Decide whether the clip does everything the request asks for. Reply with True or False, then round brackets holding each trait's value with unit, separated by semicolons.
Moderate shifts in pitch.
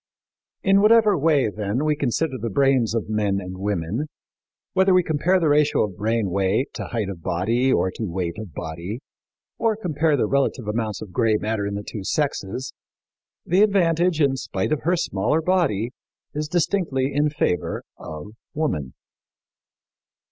False (7.5 semitones)